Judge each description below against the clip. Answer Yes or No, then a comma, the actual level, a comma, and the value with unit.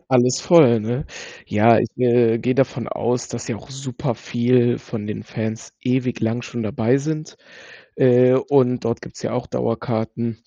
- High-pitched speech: No, low, 120 Hz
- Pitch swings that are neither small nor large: No, narrow, 1.9 semitones